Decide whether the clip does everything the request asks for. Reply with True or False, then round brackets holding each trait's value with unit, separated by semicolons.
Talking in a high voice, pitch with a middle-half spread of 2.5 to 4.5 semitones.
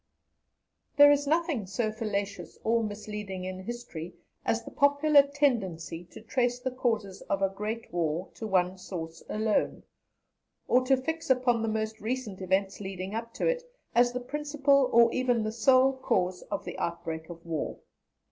False (220 Hz; 5.3 semitones)